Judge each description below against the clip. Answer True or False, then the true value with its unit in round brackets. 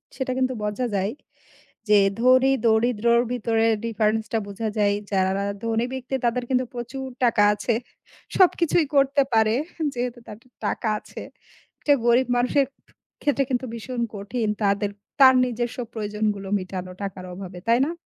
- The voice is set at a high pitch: True (230 Hz)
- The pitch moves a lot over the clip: False (3.5 semitones)